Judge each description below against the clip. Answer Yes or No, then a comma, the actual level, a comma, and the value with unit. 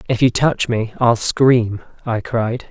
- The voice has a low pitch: Yes, low, 120 Hz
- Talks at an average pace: Yes, average, 175 wpm